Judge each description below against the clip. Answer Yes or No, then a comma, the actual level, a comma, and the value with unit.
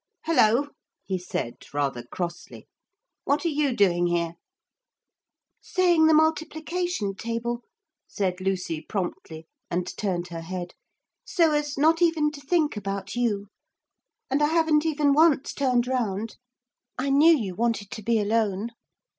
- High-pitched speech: Yes, high, 235 Hz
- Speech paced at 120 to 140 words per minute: Yes, slow, 135 wpm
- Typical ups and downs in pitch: No, wide, 8.0 semitones